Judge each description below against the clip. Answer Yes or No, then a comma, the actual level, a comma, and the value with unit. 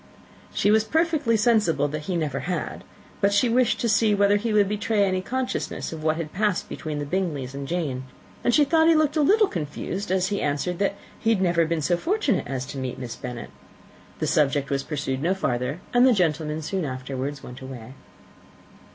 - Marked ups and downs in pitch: Yes, wide, 7.0 semitones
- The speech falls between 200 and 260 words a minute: Yes, fast, 205 wpm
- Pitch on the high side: No, medium, 180 Hz